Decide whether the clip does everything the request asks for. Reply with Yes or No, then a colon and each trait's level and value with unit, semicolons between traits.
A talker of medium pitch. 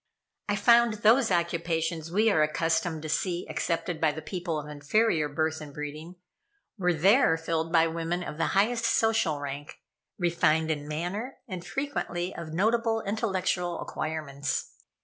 Yes: medium, 170 Hz